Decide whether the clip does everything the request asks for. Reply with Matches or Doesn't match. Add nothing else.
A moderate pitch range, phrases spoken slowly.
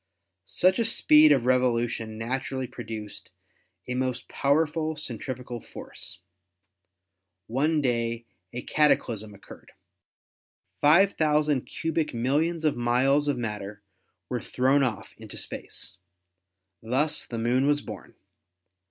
Matches